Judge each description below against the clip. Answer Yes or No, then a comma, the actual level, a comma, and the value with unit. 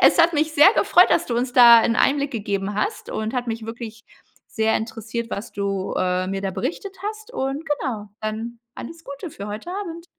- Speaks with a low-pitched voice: No, high, 235 Hz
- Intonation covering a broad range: Yes, wide, 5.9 semitones